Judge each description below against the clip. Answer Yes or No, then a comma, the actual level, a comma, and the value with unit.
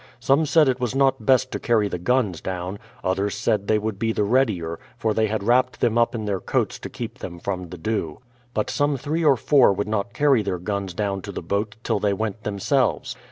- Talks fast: Yes, fast, 230 wpm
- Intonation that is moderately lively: Yes, average, 4.1 semitones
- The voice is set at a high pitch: No, low, 110 Hz